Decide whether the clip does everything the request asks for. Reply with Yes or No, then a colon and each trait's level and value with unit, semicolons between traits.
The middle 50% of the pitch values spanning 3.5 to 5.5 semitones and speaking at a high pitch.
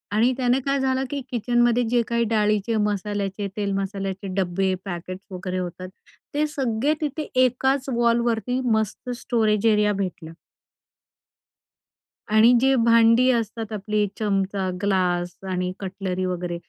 Yes: average, 3.8 semitones; high, 210 Hz